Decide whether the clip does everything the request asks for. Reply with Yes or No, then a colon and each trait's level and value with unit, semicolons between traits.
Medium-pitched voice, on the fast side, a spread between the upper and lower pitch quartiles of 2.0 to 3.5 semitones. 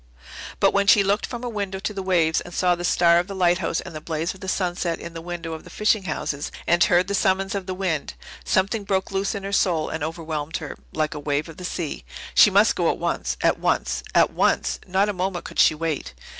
Yes: medium, 180 Hz; fast, 245 wpm; average, 3.0 semitones